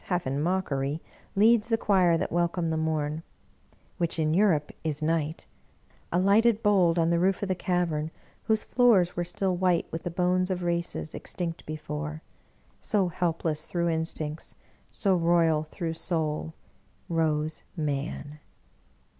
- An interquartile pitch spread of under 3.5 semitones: Yes, average, 2.7 semitones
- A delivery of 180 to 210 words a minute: No, average, 155 wpm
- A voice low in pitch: No, medium, 170 Hz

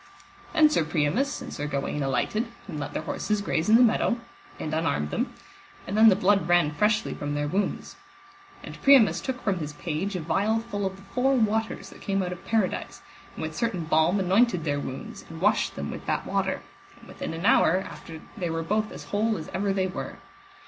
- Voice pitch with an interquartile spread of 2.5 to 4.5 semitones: No, average, 5.2 semitones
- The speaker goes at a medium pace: No, fast, 210 wpm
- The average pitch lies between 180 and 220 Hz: Yes, high, 190 Hz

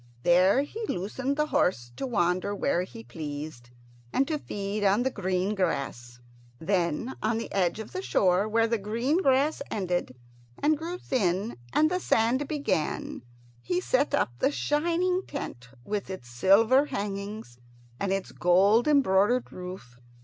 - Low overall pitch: No, high, 205 Hz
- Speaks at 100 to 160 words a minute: Yes, average, 150 wpm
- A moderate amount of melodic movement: No, wide, 6.7 semitones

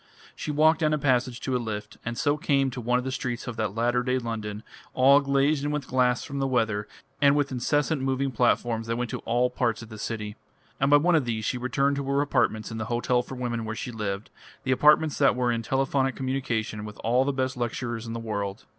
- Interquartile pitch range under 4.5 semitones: Yes, average, 3.2 semitones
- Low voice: Yes, low, 125 Hz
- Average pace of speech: No, fast, 240 wpm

